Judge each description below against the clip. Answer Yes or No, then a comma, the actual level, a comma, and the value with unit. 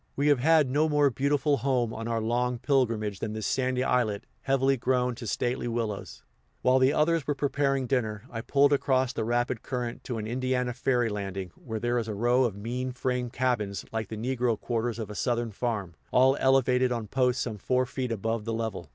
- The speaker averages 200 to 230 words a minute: Yes, fast, 205 wpm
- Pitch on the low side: Yes, low, 125 Hz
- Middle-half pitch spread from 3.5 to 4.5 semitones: No, narrow, 2.6 semitones